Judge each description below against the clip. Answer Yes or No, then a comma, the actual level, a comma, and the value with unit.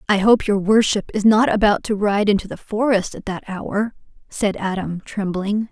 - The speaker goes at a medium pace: Yes, average, 190 wpm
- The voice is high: Yes, high, 205 Hz